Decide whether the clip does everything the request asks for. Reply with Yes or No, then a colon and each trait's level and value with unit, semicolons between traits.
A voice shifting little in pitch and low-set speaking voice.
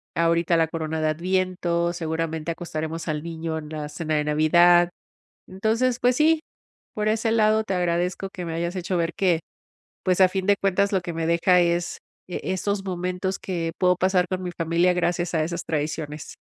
No: narrow, 2.3 semitones; medium, 175 Hz